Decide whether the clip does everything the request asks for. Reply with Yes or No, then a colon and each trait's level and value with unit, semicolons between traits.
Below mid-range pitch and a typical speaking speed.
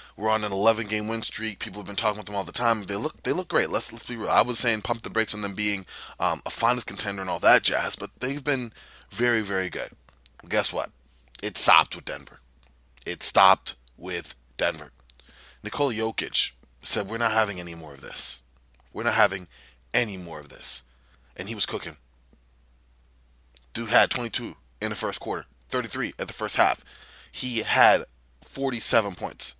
Yes: very low, 95 Hz; average, 195 wpm